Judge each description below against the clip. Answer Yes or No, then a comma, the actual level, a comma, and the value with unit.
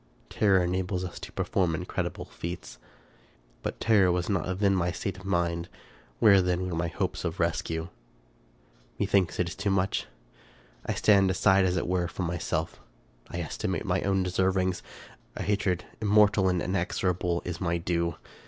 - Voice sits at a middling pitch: No, very low, 90 Hz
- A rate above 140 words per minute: Yes, average, 160 wpm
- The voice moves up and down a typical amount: No, narrow, 1.9 semitones